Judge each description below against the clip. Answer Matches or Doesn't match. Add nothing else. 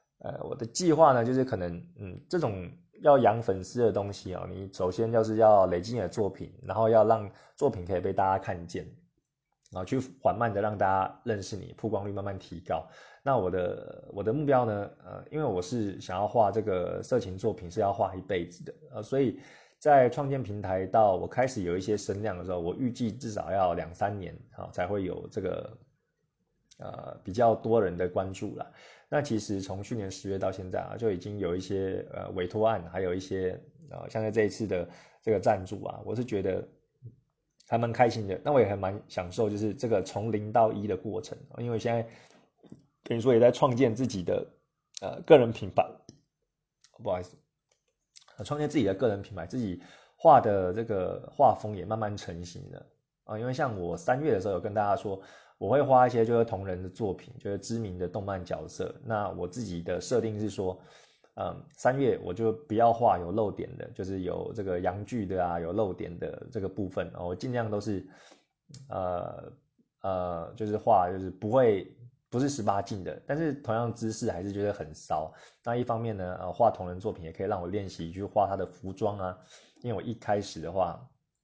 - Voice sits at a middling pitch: Doesn't match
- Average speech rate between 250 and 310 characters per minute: Matches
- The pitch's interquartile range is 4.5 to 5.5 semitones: Doesn't match